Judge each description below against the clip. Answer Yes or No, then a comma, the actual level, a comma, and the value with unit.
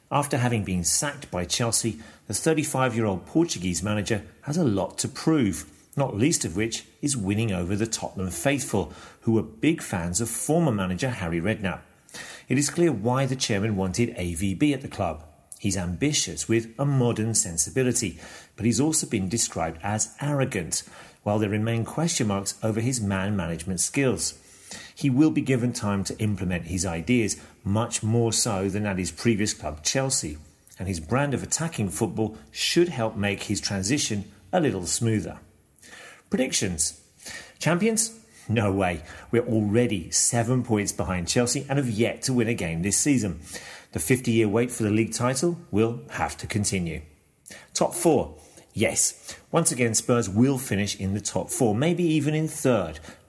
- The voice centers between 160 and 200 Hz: No, low, 110 Hz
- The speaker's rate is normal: Yes, average, 165 wpm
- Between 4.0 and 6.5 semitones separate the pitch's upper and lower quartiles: Yes, average, 5.1 semitones